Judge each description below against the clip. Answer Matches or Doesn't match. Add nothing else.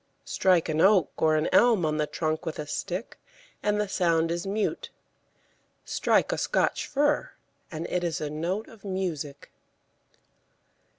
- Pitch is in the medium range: Matches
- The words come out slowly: Doesn't match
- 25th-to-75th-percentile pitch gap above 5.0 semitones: Doesn't match